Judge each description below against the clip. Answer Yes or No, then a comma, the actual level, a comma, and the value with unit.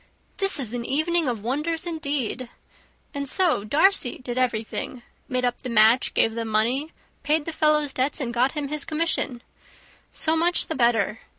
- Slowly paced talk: No, average, 170 wpm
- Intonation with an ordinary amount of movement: Yes, average, 4.6 semitones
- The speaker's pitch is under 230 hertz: No, very high, 270 Hz